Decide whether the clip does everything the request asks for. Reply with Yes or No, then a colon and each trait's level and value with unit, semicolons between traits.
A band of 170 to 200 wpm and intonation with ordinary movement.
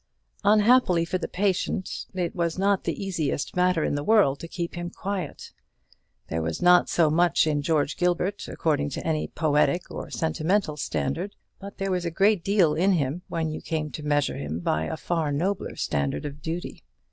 Yes: average, 185 wpm; average, 3.9 semitones